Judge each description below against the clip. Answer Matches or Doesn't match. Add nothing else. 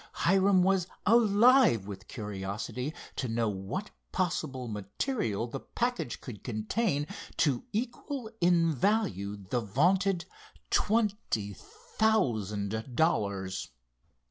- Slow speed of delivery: Matches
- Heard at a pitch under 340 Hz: Matches